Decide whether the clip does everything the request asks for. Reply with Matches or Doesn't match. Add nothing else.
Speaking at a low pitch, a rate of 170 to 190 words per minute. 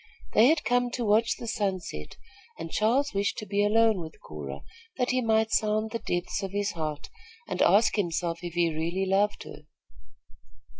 Doesn't match